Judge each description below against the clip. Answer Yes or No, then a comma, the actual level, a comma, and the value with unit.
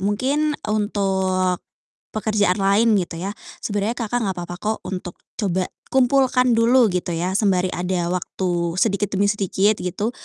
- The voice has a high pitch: Yes, high, 200 Hz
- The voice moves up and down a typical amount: Yes, average, 3.2 semitones